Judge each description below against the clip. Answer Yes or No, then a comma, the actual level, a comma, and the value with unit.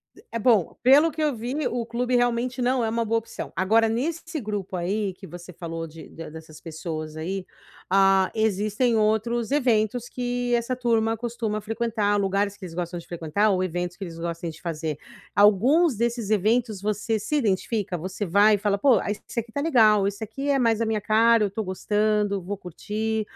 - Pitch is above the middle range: Yes, high, 215 Hz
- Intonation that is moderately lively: Yes, average, 3.8 semitones